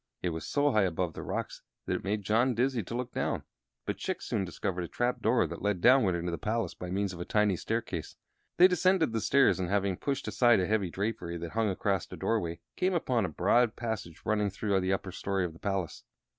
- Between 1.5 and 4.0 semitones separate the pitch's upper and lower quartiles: No, average, 4.5 semitones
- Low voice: Yes, low, 100 Hz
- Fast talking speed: Yes, fast, 230 wpm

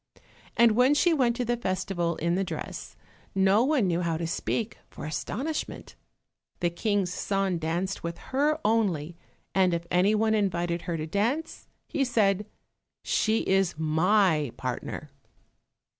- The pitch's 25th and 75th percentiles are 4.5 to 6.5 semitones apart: Yes, average, 4.9 semitones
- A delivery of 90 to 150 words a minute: Yes, average, 145 wpm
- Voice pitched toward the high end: Yes, high, 195 Hz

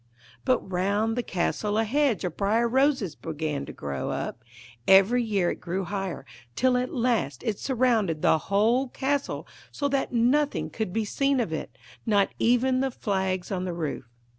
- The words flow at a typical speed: Yes, average, 170 wpm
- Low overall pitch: No, high, 215 Hz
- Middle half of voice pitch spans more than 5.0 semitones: Yes, wide, 5.4 semitones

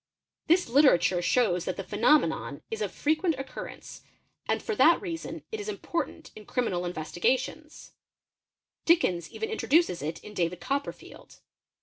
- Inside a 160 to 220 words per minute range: No, average, 140 wpm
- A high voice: Yes, very high, 265 Hz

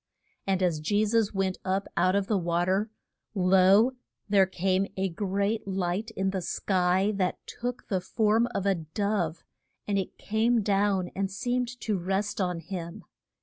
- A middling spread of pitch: No, narrow, 2.2 semitones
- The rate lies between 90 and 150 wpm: No, average, 165 wpm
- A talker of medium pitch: No, high, 195 Hz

